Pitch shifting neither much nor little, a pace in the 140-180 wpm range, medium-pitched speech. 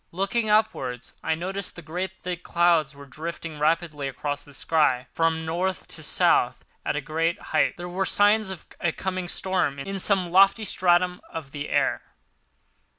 Yes: average, 3.7 semitones; average, 160 wpm; medium, 170 Hz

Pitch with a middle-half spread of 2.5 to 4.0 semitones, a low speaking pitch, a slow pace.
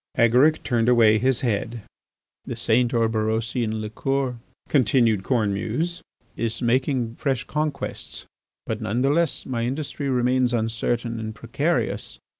Yes: average, 2.8 semitones; low, 120 Hz; slow, 120 wpm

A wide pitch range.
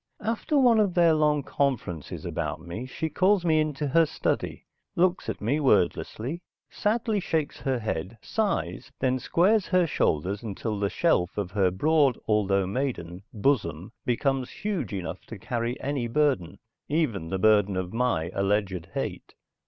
Yes: wide, 8.2 semitones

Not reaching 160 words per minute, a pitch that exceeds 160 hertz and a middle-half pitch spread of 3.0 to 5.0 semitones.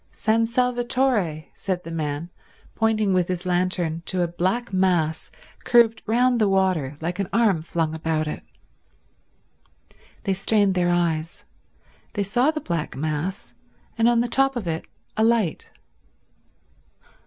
No: average, 140 wpm; medium, 185 Hz; wide, 5.4 semitones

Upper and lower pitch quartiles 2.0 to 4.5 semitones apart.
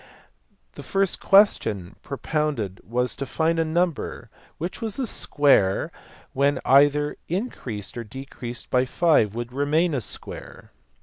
No: wide, 5.4 semitones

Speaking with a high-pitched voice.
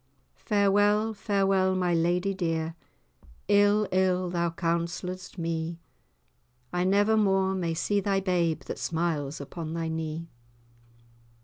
No: medium, 180 Hz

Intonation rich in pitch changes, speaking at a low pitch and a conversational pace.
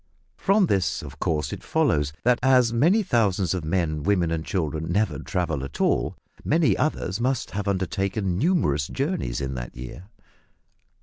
Yes: wide, 7.8 semitones; very low, 95 Hz; average, 160 wpm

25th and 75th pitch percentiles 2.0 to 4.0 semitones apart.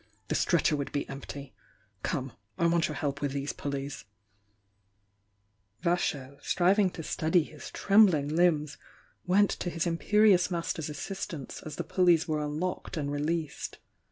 Yes: average, 3.6 semitones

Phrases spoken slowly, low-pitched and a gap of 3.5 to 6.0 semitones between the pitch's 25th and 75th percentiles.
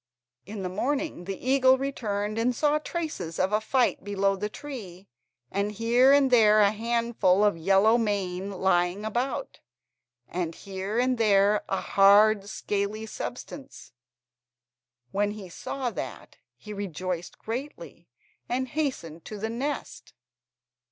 No: slow, 130 wpm; high, 210 Hz; average, 4.0 semitones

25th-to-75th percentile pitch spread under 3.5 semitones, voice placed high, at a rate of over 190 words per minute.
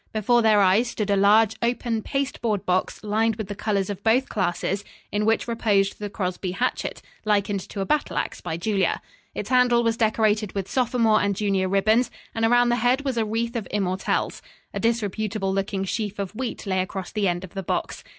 Yes: average, 2.7 semitones; high, 210 Hz; average, 200 wpm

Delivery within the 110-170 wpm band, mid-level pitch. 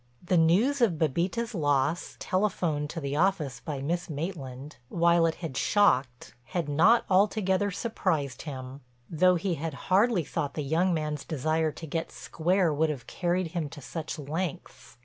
Yes: average, 160 wpm; medium, 165 Hz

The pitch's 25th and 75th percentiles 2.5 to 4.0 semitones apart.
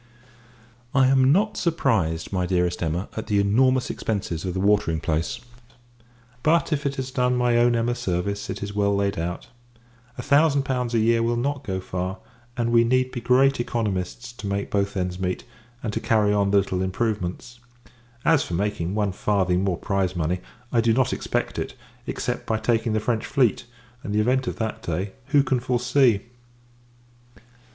No: average, 4.8 semitones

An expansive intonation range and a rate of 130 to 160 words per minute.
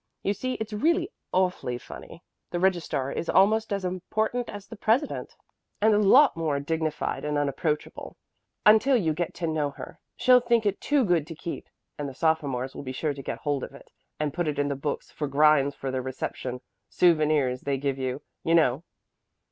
No: wide, 6.5 semitones; average, 195 wpm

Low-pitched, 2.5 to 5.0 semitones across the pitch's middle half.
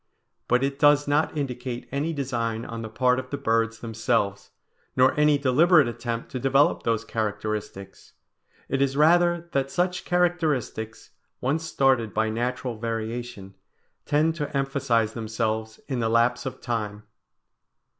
Yes: low, 125 Hz; average, 4.0 semitones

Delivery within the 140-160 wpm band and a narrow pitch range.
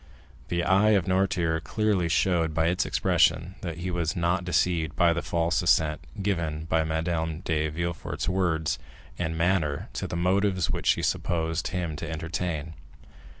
Yes: average, 155 wpm; narrow, 2.1 semitones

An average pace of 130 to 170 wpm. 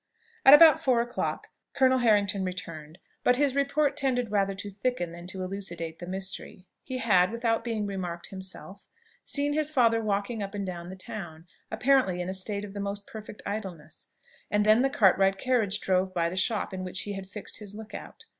No: average, 195 wpm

